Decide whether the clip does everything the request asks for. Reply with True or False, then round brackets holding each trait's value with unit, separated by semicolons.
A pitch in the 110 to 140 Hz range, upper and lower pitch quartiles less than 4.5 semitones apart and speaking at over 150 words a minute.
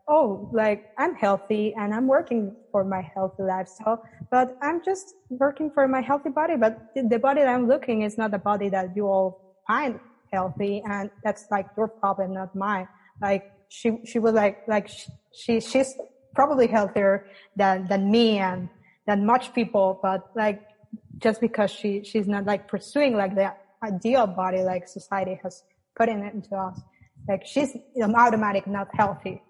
False (210 Hz; 3.1 semitones; 175 wpm)